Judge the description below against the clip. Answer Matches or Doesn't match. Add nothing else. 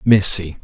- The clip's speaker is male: Matches